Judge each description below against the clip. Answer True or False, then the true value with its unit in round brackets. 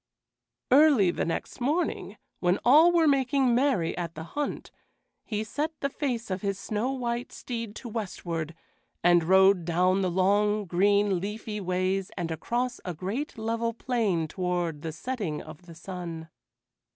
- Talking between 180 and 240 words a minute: False (150 wpm)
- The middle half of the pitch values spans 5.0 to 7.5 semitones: True (5.6 semitones)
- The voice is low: False (200 Hz)